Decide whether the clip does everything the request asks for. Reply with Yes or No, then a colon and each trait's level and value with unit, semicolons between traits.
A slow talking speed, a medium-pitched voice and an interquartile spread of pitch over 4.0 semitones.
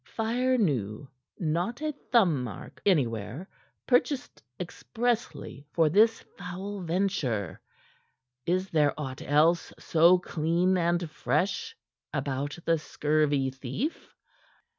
Yes: slow, 95 wpm; medium, 165 Hz; wide, 5.4 semitones